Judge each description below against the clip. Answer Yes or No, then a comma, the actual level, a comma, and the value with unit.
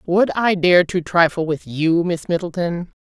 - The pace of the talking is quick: No, average, 180 wpm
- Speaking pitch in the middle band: Yes, medium, 175 Hz